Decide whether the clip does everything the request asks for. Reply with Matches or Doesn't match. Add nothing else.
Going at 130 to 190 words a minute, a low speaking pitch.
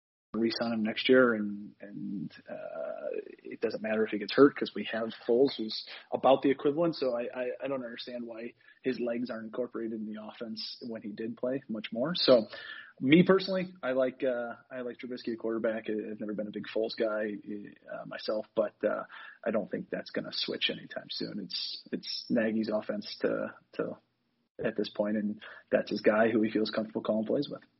Doesn't match